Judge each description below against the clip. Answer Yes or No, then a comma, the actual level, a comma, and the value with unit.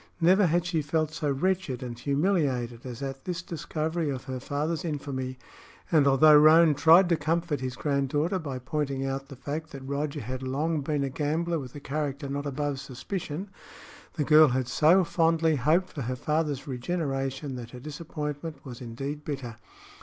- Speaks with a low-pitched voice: No, medium, 145 Hz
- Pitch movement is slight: No, average, 3.2 semitones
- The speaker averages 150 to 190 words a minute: Yes, average, 175 wpm